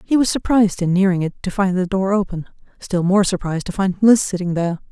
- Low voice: No, high, 190 Hz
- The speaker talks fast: Yes, fast, 220 wpm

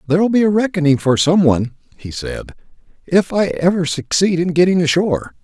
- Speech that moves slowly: No, average, 175 wpm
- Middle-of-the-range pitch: Yes, medium, 170 Hz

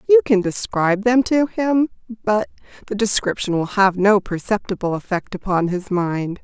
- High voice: Yes, high, 205 Hz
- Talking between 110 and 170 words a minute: Yes, average, 160 wpm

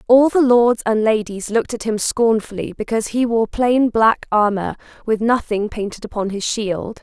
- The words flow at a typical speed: Yes, average, 180 wpm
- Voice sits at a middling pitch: No, high, 225 Hz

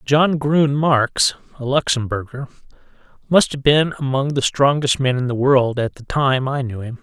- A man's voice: Yes, male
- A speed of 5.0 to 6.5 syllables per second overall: No, 4.5 syllables/s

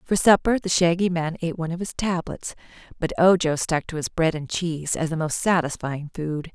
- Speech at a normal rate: No, fast, 210 wpm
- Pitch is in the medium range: Yes, medium, 165 Hz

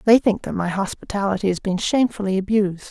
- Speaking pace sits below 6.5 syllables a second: No, 6.6 syllables/s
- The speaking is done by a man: No, female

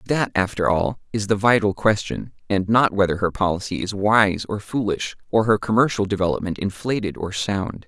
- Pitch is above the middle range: No, low, 100 Hz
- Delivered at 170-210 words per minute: Yes, average, 175 wpm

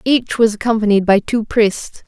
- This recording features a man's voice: No, female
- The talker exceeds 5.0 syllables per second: No, 4.6 syllables/s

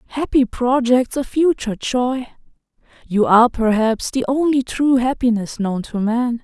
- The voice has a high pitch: Yes, high, 245 Hz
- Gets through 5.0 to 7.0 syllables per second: No, 4.4 syllables/s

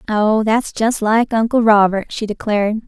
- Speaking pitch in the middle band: No, high, 220 Hz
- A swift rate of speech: No, average, 165 wpm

